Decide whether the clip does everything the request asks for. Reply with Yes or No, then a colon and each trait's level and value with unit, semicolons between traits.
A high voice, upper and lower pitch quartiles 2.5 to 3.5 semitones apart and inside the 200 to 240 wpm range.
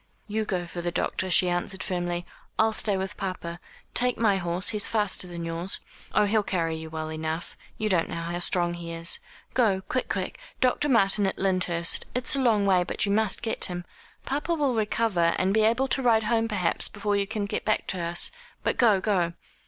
No: high, 195 Hz; average, 4.0 semitones; fast, 205 wpm